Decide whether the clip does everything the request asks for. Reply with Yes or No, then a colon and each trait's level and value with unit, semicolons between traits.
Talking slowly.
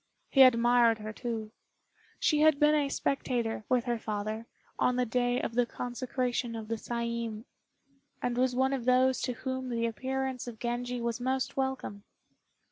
No: average, 165 wpm